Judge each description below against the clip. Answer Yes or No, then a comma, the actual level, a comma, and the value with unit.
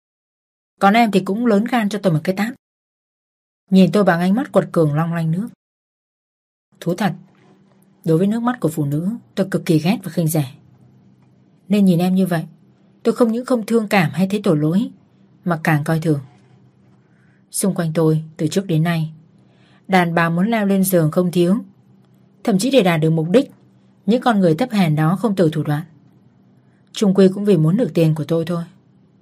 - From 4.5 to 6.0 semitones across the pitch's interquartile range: No, average, 3.8 semitones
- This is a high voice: No, medium, 180 Hz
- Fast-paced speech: No, average, 200 wpm